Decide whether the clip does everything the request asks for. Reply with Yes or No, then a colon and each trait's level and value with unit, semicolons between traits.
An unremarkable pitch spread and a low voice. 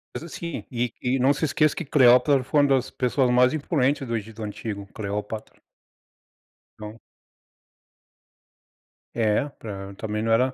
Yes: average, 4.3 semitones; low, 125 Hz